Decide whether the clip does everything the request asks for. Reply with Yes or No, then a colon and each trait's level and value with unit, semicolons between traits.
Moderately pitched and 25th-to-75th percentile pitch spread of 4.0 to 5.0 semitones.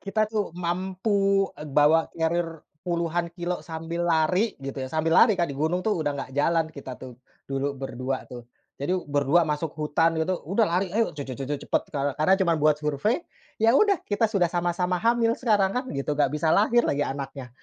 Yes: medium, 165 Hz; average, 4.7 semitones